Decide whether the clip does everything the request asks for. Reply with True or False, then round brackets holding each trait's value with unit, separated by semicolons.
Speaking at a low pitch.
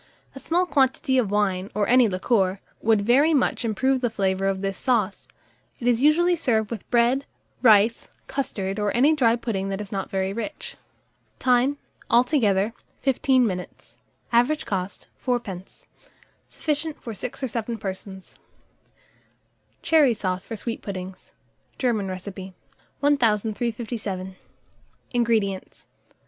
False (225 Hz)